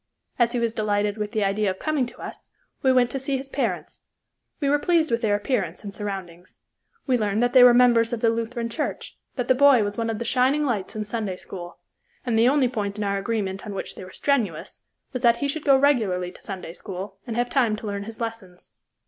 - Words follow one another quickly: Yes, fast, 235 wpm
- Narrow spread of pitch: No, average, 3.8 semitones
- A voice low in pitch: No, high, 230 Hz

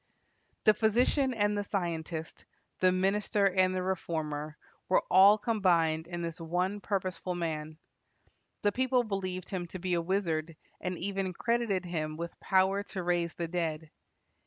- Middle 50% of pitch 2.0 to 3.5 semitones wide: Yes, average, 3.0 semitones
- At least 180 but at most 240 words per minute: No, average, 150 wpm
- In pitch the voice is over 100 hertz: Yes, medium, 185 Hz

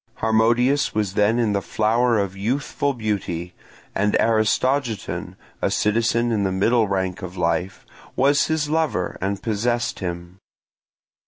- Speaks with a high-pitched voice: No, low, 110 Hz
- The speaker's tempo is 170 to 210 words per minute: No, slow, 135 wpm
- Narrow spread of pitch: No, average, 3.8 semitones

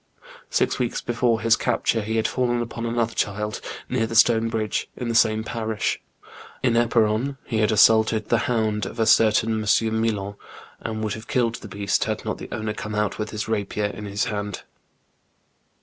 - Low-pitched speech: Yes, low, 110 Hz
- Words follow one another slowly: No, average, 185 wpm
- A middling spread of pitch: No, narrow, 1.5 semitones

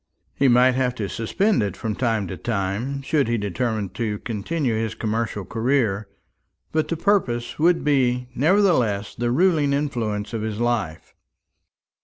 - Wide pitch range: No, average, 4.6 semitones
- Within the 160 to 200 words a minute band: No, average, 150 wpm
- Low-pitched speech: Yes, low, 120 Hz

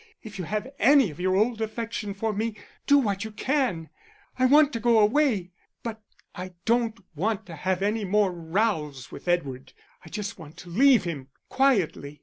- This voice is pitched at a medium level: No, high, 210 Hz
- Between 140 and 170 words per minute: No, average, 180 wpm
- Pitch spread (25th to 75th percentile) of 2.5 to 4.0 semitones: No, average, 4.6 semitones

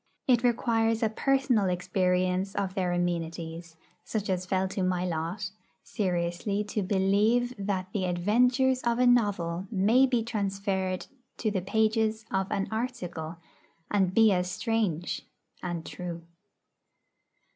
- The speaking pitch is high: Yes, high, 195 Hz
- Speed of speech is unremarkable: No, slow, 130 wpm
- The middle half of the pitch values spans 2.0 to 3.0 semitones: No, average, 3.7 semitones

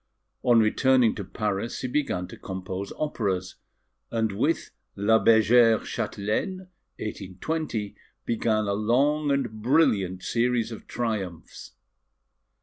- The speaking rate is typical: No, slow, 110 wpm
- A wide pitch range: No, average, 3.7 semitones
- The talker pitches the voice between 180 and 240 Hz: No, low, 110 Hz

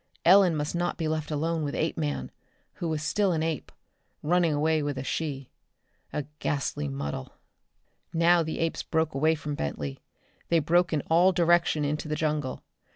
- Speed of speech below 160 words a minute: No, average, 165 wpm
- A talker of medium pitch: Yes, medium, 155 Hz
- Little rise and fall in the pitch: Yes, narrow, 2.3 semitones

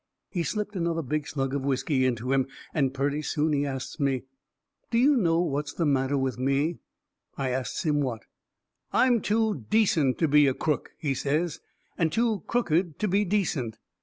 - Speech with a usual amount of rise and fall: Yes, average, 4.6 semitones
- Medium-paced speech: Yes, average, 180 wpm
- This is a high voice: No, medium, 150 Hz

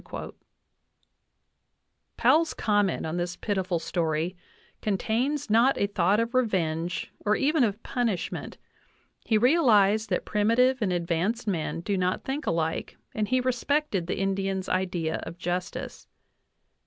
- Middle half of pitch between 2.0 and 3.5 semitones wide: No, average, 5.0 semitones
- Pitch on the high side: Yes, high, 200 Hz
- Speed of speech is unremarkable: No, slow, 130 wpm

